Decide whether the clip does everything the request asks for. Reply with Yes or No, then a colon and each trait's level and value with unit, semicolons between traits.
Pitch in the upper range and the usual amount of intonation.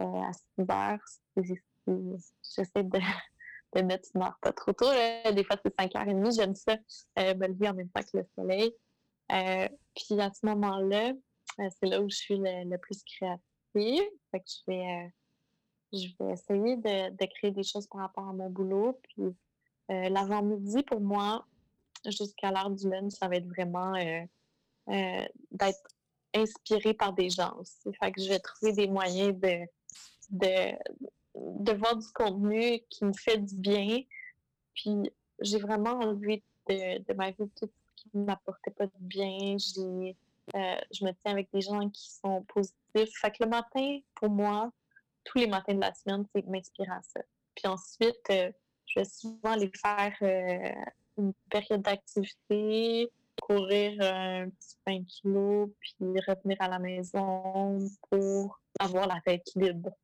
No: high, 195 Hz; narrow, 2.0 semitones